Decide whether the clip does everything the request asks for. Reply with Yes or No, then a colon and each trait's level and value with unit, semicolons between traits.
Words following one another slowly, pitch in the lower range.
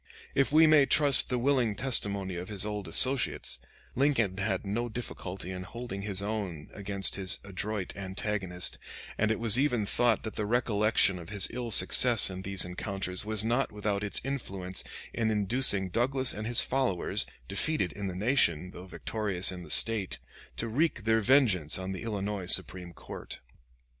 No: average, 170 wpm; low, 105 Hz